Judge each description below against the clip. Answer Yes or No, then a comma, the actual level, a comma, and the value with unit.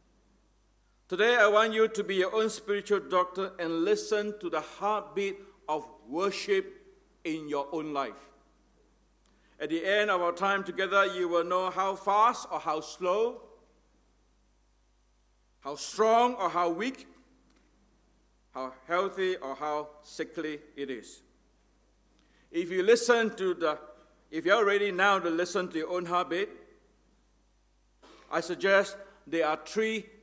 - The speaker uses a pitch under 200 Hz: Yes, high, 190 Hz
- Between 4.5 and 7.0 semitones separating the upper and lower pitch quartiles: Yes, average, 5.0 semitones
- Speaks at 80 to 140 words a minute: Yes, slow, 135 wpm